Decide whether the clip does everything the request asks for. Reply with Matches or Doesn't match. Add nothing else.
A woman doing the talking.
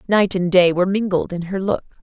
Matches